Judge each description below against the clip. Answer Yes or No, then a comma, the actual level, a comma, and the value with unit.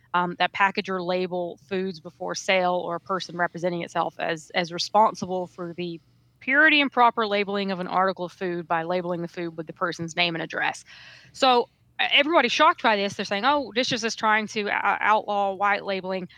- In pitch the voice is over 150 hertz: Yes, medium, 185 Hz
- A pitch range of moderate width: Yes, average, 3.3 semitones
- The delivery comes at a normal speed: Yes, average, 195 wpm